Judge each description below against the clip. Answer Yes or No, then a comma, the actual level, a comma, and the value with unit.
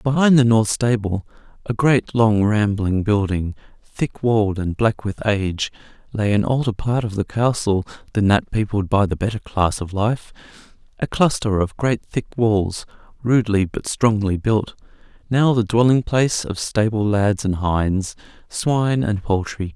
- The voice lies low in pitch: Yes, low, 110 Hz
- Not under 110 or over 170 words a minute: Yes, average, 160 wpm